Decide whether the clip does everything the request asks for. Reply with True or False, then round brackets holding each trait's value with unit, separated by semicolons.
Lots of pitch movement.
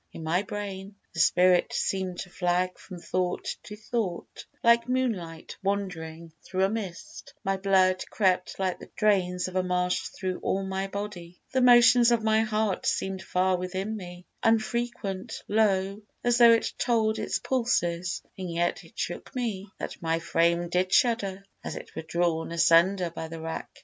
False (3.4 semitones)